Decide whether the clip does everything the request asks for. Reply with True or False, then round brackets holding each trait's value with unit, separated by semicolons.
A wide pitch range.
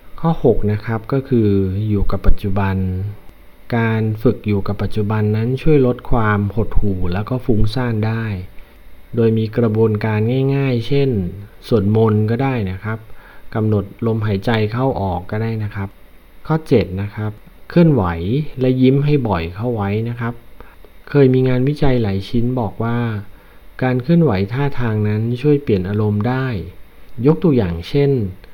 False (3.9 semitones)